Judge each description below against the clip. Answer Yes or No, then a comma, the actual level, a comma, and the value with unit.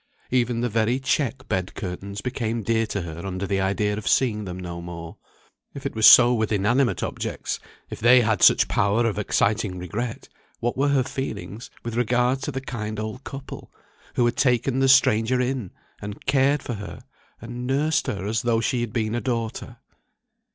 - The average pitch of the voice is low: Yes, low, 115 Hz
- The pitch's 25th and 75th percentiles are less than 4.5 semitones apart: Yes, average, 3.5 semitones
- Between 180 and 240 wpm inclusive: Yes, average, 185 wpm